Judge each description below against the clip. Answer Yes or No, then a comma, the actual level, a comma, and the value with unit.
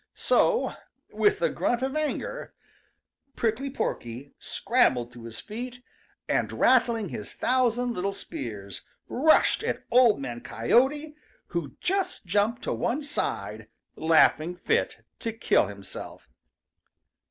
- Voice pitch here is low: No, high, 230 Hz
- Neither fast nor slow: No, slow, 120 wpm